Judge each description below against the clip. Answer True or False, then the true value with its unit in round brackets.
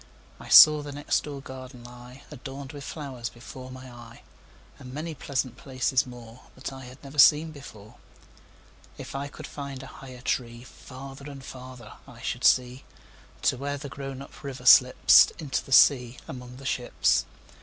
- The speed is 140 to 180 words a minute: True (145 wpm)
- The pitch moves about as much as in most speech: False (1.9 semitones)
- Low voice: True (130 Hz)